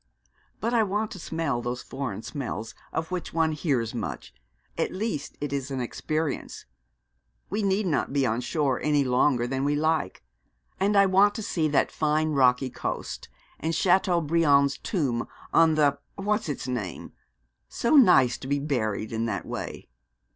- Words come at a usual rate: Yes, average, 160 wpm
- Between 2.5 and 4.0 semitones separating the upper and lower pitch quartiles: No, average, 5.2 semitones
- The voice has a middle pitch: Yes, medium, 150 Hz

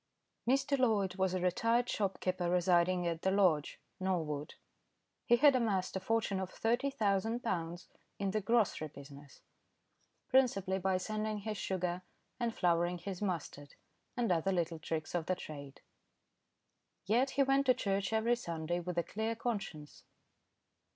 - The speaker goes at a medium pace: Yes, average, 145 wpm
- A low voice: No, high, 190 Hz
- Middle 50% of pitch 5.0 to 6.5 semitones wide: No, average, 4.5 semitones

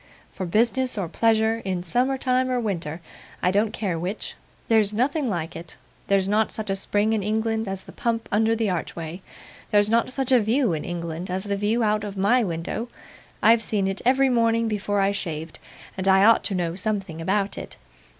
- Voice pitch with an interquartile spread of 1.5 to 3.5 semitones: Yes, average, 3.2 semitones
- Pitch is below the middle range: No, high, 210 Hz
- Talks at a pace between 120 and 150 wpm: No, average, 200 wpm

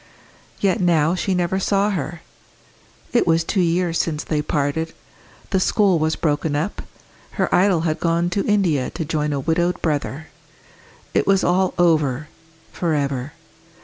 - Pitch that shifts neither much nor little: Yes, average, 3.3 semitones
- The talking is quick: No, average, 150 wpm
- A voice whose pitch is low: No, medium, 165 Hz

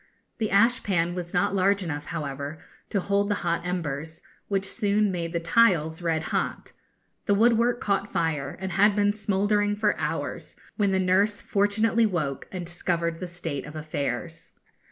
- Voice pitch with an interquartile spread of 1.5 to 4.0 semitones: Yes, average, 3.7 semitones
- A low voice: No, medium, 185 Hz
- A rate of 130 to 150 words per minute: No, average, 160 wpm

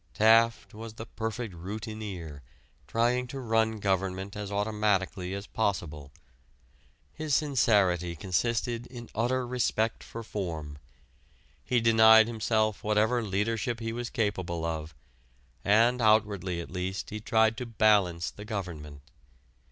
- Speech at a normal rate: No, slow, 120 wpm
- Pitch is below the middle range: Yes, low, 110 Hz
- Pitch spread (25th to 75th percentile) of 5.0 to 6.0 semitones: No, average, 3.4 semitones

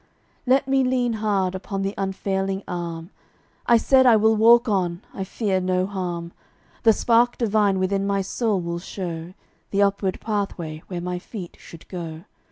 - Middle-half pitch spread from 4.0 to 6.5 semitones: No, average, 3.4 semitones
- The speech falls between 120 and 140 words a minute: No, average, 165 wpm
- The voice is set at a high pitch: Yes, high, 195 Hz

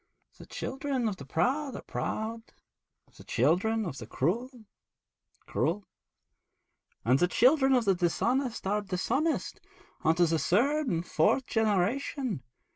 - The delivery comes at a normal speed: No, slow, 125 wpm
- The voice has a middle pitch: No, high, 220 Hz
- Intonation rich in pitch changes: Yes, wide, 6.8 semitones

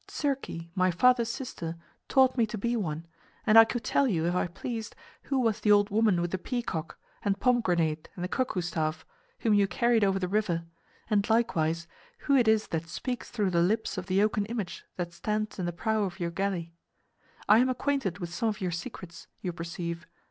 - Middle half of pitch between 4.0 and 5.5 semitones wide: Yes, average, 4.7 semitones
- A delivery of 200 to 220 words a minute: Yes, fast, 205 wpm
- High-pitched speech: Yes, high, 200 Hz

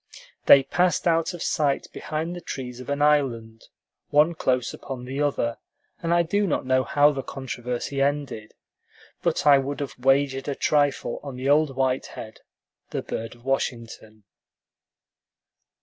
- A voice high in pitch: No, low, 135 Hz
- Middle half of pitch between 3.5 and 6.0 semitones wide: No, average, 2.7 semitones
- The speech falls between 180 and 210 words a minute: No, average, 155 wpm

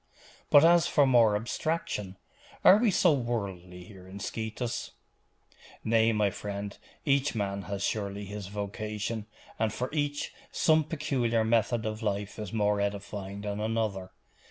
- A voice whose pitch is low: Yes, low, 110 Hz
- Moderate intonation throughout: Yes, average, 3.2 semitones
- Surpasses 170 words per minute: No, average, 140 wpm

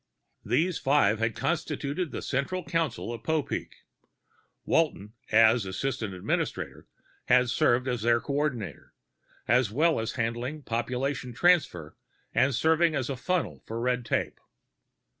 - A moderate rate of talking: No, slow, 125 wpm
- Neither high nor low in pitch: No, low, 125 Hz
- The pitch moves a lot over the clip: No, average, 4.8 semitones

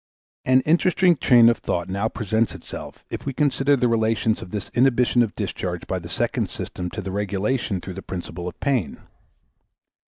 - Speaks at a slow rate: No, average, 175 wpm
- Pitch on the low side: Yes, low, 115 Hz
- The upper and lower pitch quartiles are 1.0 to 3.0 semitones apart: No, average, 5.0 semitones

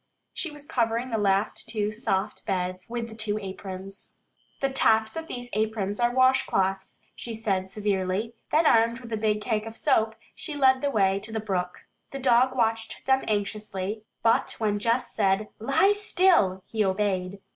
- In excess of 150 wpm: Yes, average, 170 wpm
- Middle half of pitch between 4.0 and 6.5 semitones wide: No, average, 3.5 semitones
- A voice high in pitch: Yes, high, 220 Hz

